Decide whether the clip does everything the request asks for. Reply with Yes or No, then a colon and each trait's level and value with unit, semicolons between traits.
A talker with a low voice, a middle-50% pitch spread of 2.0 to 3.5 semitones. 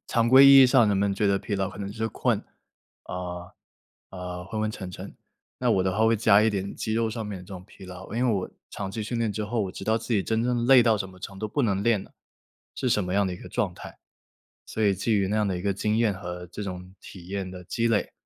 Yes: low, 100 Hz; average, 2.9 semitones